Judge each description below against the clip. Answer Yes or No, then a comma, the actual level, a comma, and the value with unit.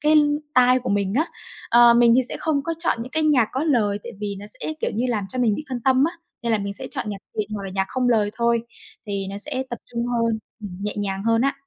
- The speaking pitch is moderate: No, high, 235 Hz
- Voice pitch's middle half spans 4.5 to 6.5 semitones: No, average, 3.9 semitones